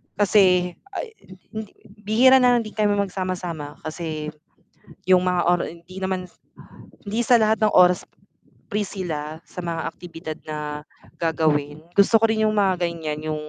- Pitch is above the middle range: No, medium, 180 Hz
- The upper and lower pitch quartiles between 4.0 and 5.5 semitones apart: Yes, average, 4.6 semitones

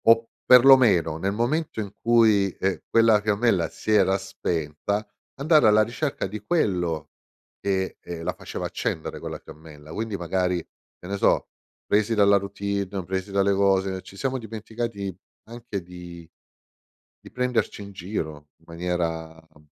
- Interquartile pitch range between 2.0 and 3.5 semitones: No, average, 4.0 semitones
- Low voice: Yes, low, 100 Hz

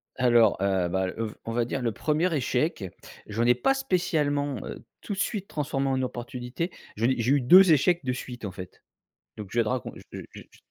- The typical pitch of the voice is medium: No, low, 125 Hz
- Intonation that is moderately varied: Yes, average, 4.7 semitones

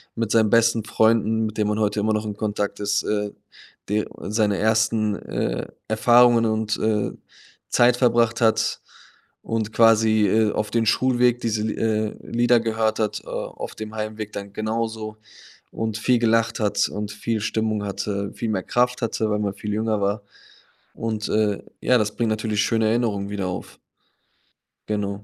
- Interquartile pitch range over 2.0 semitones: No, narrow, 1.3 semitones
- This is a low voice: Yes, low, 110 Hz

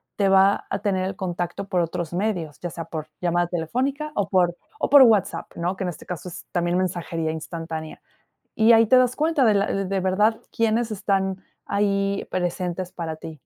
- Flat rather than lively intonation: No, average, 3.1 semitones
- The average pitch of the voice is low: No, medium, 185 Hz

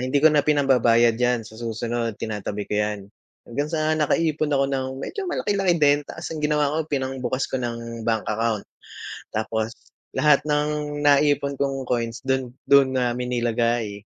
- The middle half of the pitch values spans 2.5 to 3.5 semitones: No, average, 4.1 semitones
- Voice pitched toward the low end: Yes, low, 130 Hz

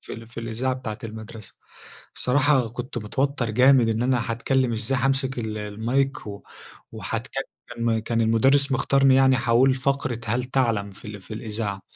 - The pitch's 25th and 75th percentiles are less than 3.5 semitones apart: Yes, average, 3.0 semitones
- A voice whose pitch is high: No, low, 120 Hz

